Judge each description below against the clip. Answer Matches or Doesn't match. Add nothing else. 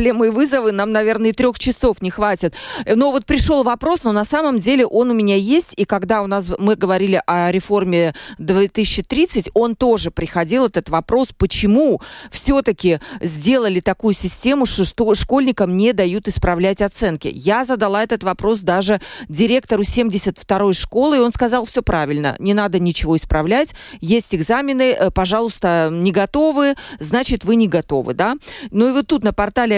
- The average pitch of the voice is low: Doesn't match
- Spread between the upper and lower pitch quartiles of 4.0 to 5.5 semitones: Matches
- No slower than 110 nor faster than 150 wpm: Doesn't match